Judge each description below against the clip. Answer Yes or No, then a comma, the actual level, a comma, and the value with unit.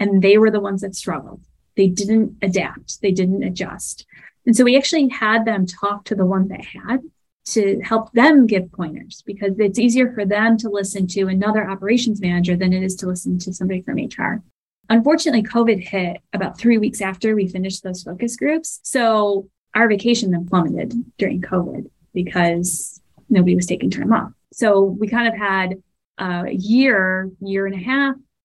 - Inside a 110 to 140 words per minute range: No, average, 180 wpm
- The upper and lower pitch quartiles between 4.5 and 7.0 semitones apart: No, average, 3.3 semitones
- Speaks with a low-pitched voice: No, high, 200 Hz